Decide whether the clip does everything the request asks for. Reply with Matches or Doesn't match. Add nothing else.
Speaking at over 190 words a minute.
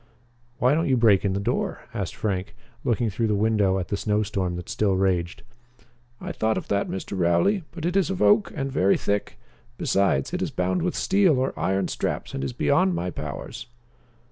Matches